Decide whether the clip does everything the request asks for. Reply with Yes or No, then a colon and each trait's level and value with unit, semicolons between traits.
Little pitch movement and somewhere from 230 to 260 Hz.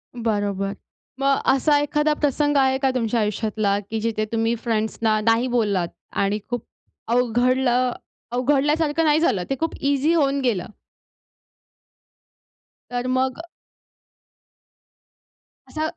No: average, 4.2 semitones; high, 245 Hz